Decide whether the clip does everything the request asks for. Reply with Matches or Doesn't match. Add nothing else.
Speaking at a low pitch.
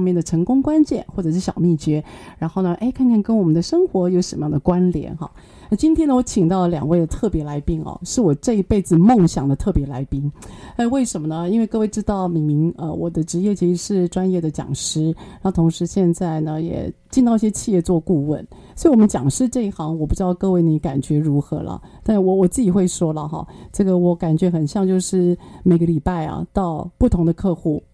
Doesn't match